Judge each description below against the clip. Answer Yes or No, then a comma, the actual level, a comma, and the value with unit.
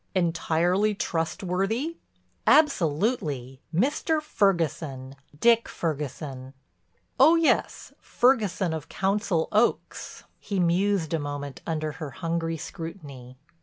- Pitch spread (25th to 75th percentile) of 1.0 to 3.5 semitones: No, wide, 5.5 semitones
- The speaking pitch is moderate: Yes, medium, 170 Hz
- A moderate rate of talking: No, slow, 90 wpm